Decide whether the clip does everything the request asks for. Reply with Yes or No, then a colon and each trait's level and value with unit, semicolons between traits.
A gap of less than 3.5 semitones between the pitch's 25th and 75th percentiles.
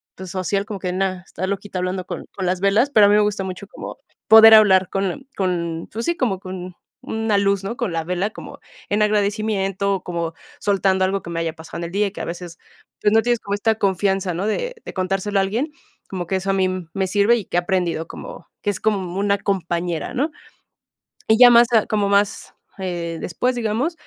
Yes: narrow, 2.5 semitones